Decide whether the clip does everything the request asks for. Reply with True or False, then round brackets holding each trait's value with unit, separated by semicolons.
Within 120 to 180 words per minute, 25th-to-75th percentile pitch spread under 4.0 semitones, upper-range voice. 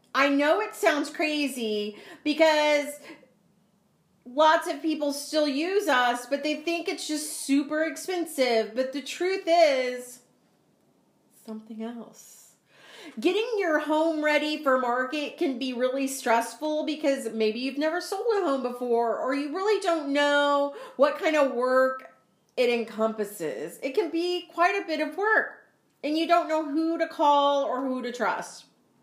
False (150 wpm; 4.3 semitones; 290 Hz)